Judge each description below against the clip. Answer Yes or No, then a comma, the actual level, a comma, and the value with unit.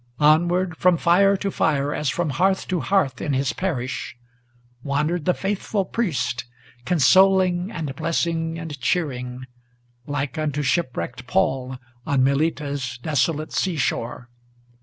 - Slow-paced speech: Yes, slow, 125 wpm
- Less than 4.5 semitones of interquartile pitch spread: No, average, 4.8 semitones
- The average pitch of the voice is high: No, medium, 155 Hz